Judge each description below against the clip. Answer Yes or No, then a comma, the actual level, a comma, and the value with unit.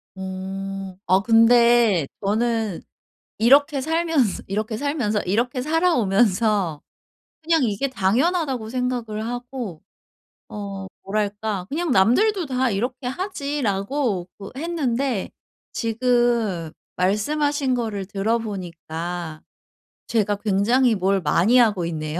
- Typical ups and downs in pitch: Yes, average, 4.8 semitones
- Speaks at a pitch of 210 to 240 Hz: Yes, high, 225 Hz